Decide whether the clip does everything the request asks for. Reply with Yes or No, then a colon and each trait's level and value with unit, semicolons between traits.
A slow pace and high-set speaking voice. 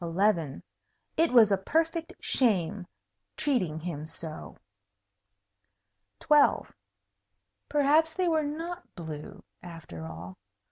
Yes: slow, 90 wpm; high, 220 Hz